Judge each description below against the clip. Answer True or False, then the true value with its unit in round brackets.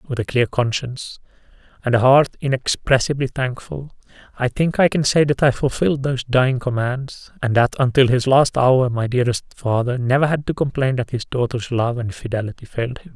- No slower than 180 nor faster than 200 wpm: True (185 wpm)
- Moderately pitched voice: False (130 Hz)